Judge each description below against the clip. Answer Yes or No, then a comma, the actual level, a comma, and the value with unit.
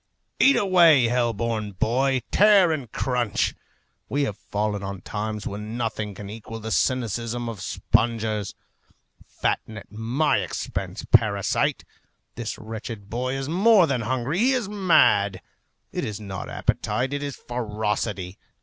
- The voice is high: No, low, 115 Hz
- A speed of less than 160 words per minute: Yes, average, 140 wpm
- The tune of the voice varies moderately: Yes, average, 4.4 semitones